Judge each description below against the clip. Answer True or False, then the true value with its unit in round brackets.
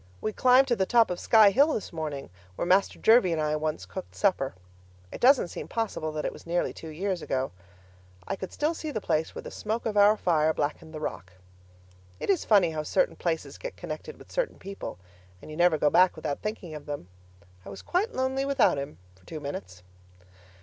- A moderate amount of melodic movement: False (6.9 semitones)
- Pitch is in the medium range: True (180 Hz)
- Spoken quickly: True (210 wpm)